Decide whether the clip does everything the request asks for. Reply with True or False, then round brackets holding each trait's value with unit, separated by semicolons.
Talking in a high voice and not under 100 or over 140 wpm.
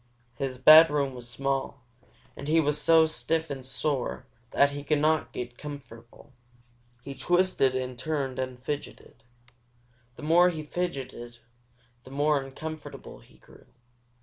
False (140 Hz; 135 wpm)